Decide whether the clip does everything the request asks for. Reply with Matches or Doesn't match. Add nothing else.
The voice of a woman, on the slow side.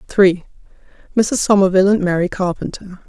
Matches